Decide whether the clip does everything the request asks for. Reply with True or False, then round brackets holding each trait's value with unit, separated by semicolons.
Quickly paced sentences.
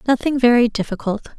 False (130 wpm)